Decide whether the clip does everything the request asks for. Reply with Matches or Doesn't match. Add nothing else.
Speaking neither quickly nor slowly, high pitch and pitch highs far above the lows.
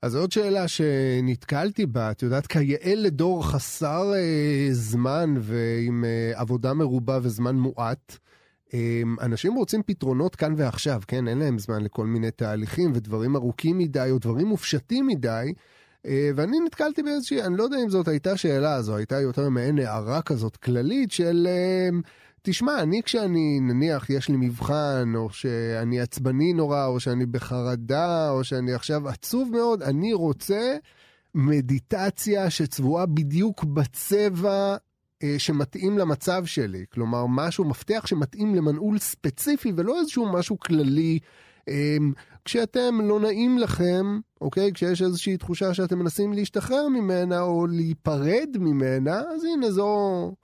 Doesn't match